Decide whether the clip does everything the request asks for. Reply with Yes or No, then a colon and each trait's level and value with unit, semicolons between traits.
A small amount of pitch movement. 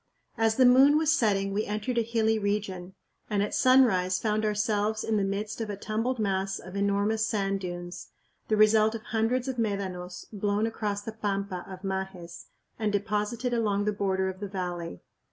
Yes: narrow, 2.3 semitones